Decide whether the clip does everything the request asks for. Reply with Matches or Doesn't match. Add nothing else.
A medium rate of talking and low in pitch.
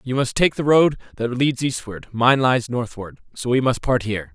Doesn't match